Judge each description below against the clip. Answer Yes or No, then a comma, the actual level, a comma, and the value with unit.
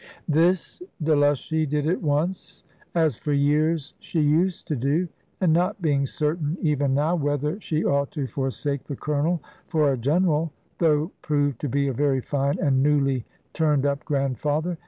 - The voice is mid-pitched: Yes, medium, 150 Hz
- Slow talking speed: No, average, 160 wpm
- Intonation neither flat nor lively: No, narrow, 2.2 semitones